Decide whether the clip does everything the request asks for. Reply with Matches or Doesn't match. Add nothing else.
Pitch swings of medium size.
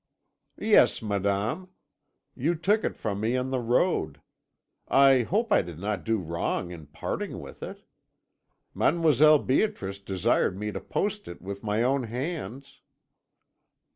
Doesn't match